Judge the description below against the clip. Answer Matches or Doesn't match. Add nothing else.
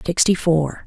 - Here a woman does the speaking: Matches